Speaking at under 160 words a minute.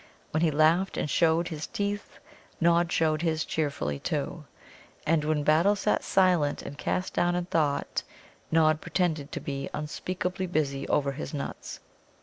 Yes: average, 150 wpm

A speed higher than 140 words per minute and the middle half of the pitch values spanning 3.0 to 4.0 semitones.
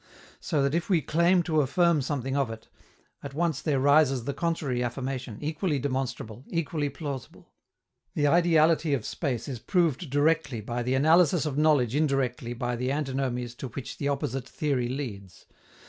Yes: average, 160 wpm; average, 3.6 semitones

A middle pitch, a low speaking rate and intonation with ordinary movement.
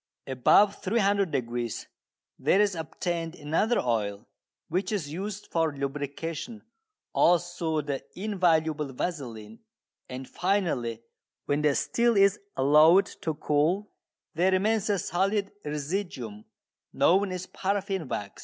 No: medium, 165 Hz; slow, 110 wpm; wide, 5.7 semitones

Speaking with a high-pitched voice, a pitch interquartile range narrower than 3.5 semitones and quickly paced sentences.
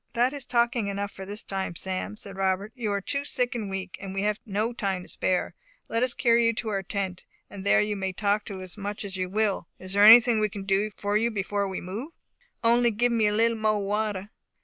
Yes: high, 205 Hz; average, 2.9 semitones; fast, 240 wpm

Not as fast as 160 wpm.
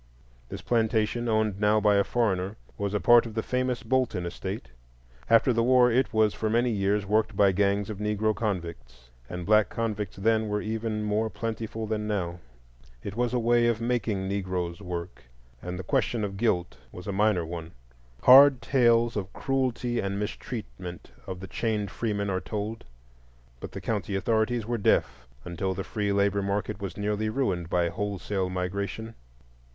No: average, 170 wpm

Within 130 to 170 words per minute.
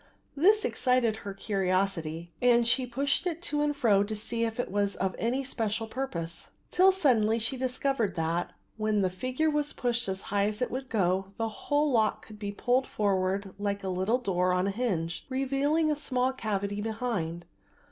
No: average, 185 wpm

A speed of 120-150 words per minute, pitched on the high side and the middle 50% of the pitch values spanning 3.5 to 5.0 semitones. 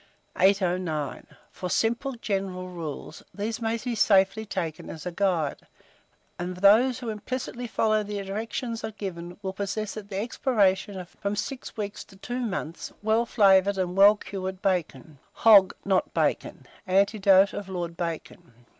No: average, 145 wpm; high, 195 Hz; average, 3.0 semitones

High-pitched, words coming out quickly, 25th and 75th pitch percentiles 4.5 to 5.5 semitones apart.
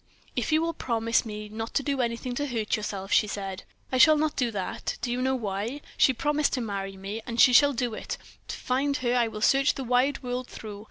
No: high, 240 Hz; fast, 235 wpm; average, 4.1 semitones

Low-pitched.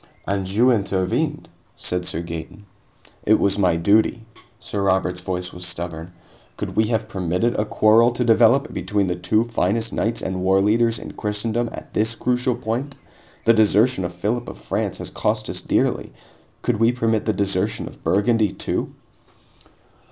Yes: low, 105 Hz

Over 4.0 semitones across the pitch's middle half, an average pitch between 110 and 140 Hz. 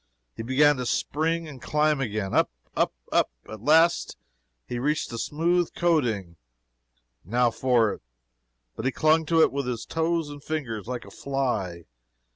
Yes: average, 5.1 semitones; low, 135 Hz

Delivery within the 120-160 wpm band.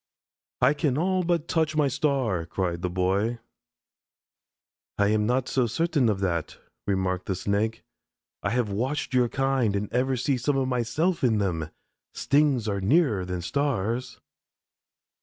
Yes: average, 150 wpm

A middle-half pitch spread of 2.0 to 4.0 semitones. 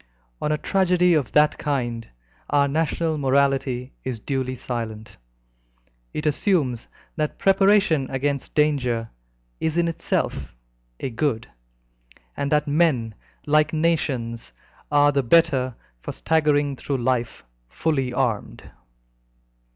Yes: average, 3.5 semitones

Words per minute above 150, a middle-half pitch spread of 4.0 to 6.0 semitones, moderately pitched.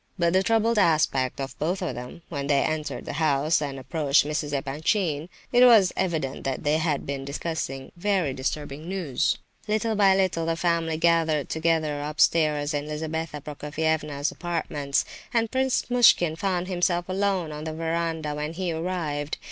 No: average, 160 wpm; average, 3.2 semitones; medium, 160 Hz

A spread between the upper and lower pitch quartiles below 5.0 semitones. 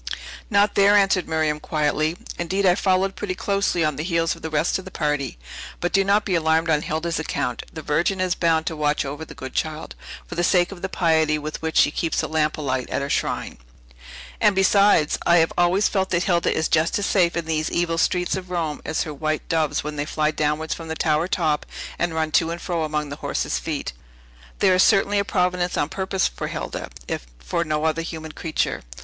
Yes: average, 2.9 semitones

